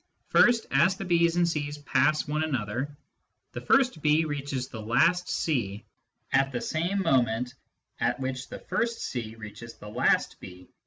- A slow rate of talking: No, average, 160 wpm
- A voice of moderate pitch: Yes, medium, 145 Hz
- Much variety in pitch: Yes, wide, 5.9 semitones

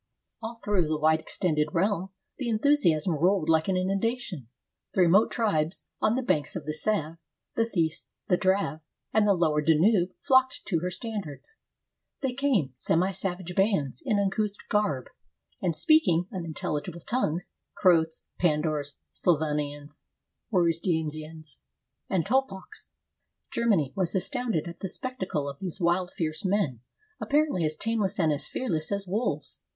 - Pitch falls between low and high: Yes, medium, 180 Hz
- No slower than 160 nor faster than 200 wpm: No, average, 145 wpm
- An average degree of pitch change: Yes, average, 5.0 semitones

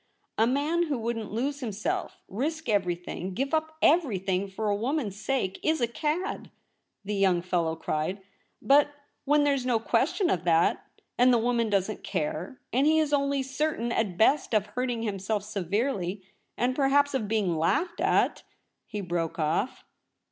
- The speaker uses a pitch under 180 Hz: No, high, 230 Hz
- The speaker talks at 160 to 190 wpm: Yes, average, 170 wpm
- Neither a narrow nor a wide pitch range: No, wide, 6.4 semitones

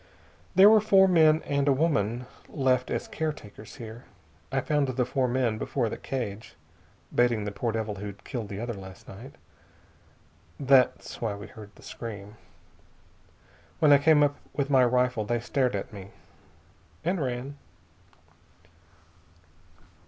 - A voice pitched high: No, low, 125 Hz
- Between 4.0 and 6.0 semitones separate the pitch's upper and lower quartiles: Yes, average, 4.5 semitones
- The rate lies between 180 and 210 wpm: No, average, 145 wpm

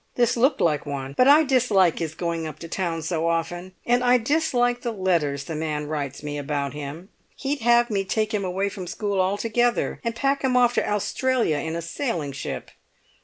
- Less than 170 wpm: No, average, 200 wpm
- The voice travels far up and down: Yes, wide, 7.3 semitones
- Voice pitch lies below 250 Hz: Yes, high, 190 Hz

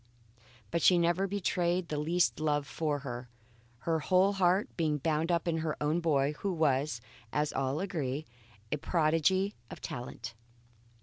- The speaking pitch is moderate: Yes, medium, 160 Hz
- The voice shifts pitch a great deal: No, average, 3.0 semitones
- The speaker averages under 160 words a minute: Yes, average, 145 wpm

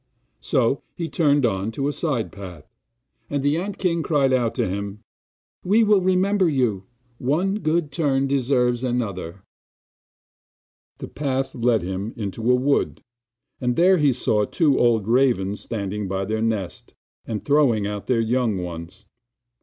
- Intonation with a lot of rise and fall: Yes, wide, 5.8 semitones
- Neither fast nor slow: Yes, average, 150 wpm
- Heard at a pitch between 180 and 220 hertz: No, low, 125 Hz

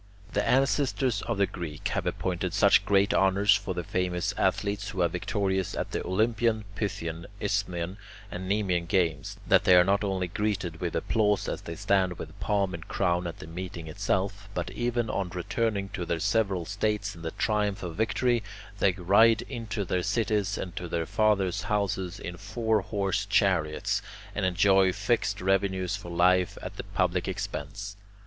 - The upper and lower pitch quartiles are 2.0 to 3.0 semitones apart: Yes, narrow, 2.6 semitones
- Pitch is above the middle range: No, low, 100 Hz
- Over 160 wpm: Yes, average, 170 wpm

